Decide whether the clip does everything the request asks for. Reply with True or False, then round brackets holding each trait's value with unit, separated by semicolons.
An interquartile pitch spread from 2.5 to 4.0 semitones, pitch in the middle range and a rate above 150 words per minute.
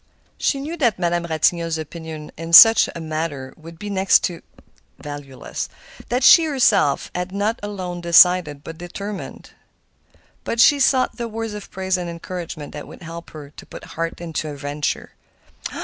False (4.4 semitones; 170 Hz; 165 wpm)